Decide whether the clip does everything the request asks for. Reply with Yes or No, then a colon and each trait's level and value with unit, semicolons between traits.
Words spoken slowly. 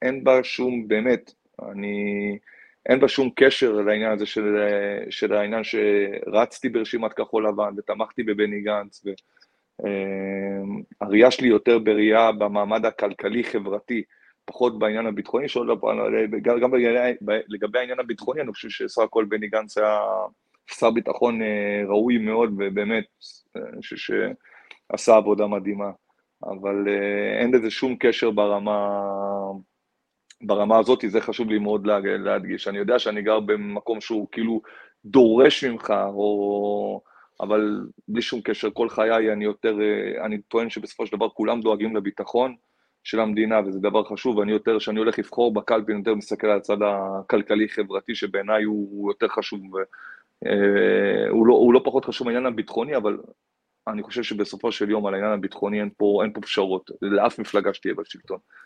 No: average, 140 wpm